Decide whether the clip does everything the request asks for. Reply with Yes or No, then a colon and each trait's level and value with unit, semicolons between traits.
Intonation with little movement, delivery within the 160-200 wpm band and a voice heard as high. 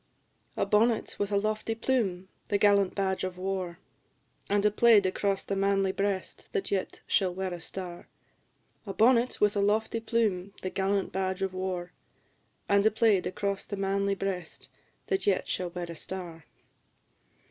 Yes: narrow, 1.9 semitones; average, 165 wpm; high, 195 Hz